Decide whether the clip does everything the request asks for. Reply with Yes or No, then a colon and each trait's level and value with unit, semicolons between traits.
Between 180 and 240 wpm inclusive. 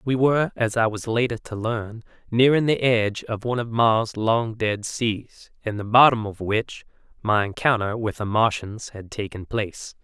Yes: average, 185 wpm